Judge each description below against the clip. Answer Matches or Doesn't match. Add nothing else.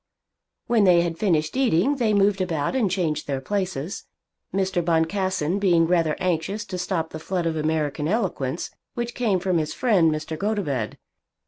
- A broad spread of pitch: Doesn't match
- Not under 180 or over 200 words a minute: Doesn't match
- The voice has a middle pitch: Matches